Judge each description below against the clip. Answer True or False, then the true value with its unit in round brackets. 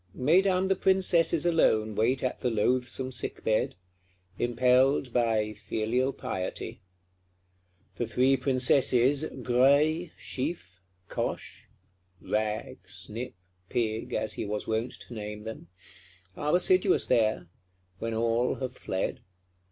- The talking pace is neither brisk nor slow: False (115 wpm)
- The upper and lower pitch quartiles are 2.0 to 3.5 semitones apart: False (4.0 semitones)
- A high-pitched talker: False (125 Hz)